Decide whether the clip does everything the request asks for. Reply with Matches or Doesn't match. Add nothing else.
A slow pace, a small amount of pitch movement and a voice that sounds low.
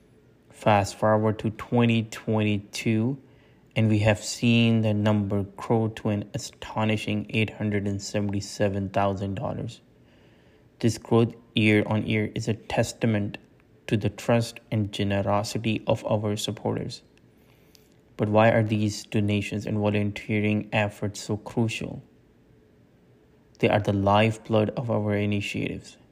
Matches